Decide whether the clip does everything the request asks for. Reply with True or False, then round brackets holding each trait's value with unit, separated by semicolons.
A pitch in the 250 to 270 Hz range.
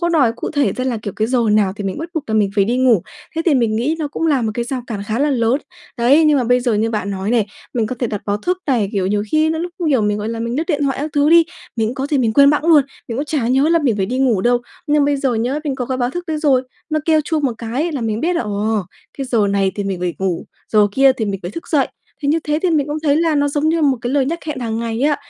True (255 Hz)